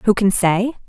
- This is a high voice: Yes, high, 205 Hz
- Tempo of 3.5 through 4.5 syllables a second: Yes, 4.2 syllables/s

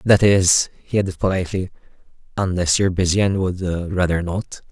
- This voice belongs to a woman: No, male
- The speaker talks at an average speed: Yes, average, 155 wpm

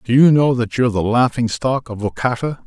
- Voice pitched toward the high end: No, low, 120 Hz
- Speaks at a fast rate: Yes, fast, 225 wpm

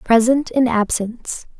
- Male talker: No, female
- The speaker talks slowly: Yes, slow, 115 wpm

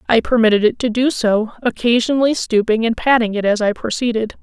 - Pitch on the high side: Yes, high, 230 Hz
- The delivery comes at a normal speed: Yes, average, 190 wpm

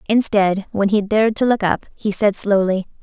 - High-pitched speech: Yes, high, 205 Hz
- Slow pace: No, average, 200 wpm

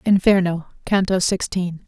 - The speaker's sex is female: Yes, female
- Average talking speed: No, slow, 95 wpm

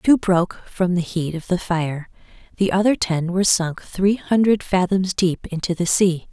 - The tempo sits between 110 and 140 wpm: No, average, 190 wpm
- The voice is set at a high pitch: No, medium, 180 Hz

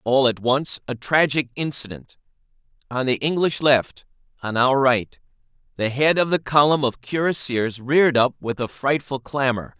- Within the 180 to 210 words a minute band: No, average, 160 wpm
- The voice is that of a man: Yes, male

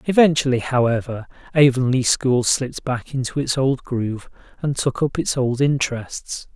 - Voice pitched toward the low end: Yes, low, 130 Hz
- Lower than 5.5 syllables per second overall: Yes, 4.8 syllables/s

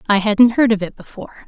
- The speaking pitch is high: Yes, high, 220 Hz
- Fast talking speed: Yes, fast, 245 wpm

